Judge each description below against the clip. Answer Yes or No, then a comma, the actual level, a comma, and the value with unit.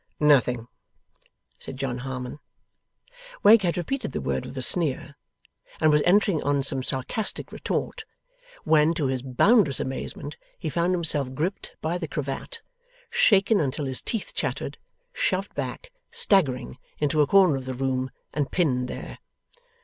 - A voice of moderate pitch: Yes, medium, 150 Hz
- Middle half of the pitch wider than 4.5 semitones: Yes, wide, 5.6 semitones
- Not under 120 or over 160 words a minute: Yes, average, 145 wpm